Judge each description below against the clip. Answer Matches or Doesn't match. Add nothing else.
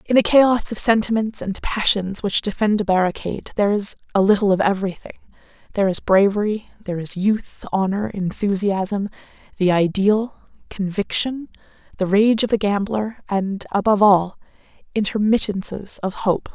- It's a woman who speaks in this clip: Matches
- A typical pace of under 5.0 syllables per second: Doesn't match